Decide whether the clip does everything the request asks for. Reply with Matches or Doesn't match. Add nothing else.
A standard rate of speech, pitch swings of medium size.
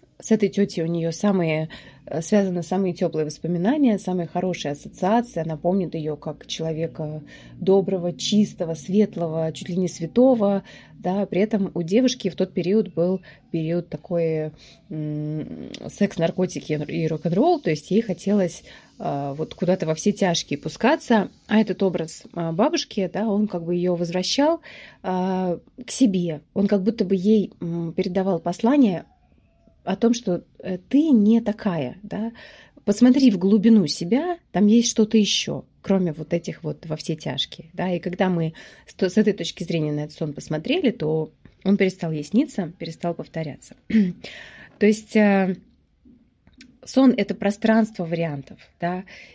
Matches